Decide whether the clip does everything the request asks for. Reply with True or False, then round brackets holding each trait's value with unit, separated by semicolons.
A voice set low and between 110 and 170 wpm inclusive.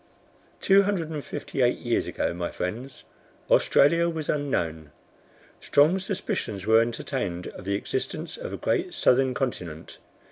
True (125 Hz; 140 wpm)